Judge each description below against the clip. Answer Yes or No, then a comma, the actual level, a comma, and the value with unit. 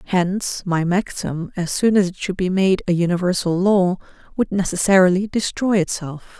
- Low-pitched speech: No, medium, 185 Hz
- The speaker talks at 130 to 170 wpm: Yes, average, 160 wpm